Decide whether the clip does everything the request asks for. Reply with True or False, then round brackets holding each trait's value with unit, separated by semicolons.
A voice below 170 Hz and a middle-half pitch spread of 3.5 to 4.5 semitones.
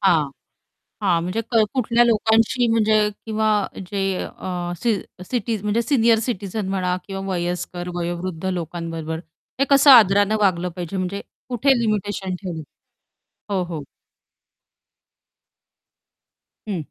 False (195 Hz; 4.0 semitones)